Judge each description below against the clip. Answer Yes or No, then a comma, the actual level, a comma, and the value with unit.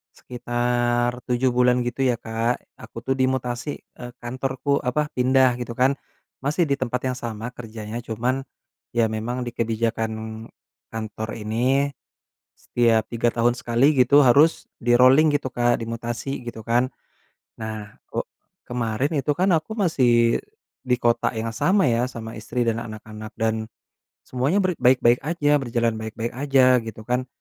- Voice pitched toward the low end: Yes, low, 120 Hz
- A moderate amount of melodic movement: No, narrow, 2.3 semitones